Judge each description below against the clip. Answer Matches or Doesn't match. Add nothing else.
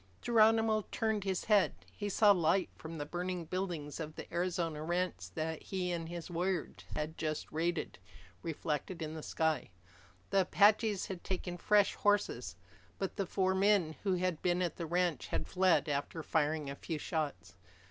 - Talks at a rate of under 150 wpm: Doesn't match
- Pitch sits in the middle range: Matches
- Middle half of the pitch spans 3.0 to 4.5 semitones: Matches